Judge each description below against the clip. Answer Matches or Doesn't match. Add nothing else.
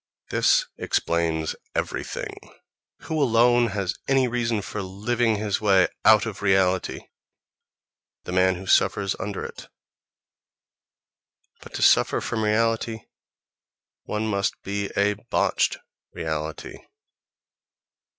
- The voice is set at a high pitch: Doesn't match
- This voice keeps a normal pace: Doesn't match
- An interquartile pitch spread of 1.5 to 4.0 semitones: Matches